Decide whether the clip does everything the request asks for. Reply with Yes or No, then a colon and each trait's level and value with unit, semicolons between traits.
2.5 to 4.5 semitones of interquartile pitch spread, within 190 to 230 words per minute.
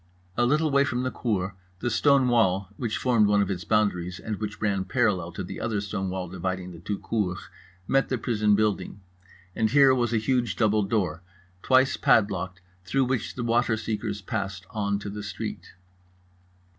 No: average, 4.0 semitones; average, 180 wpm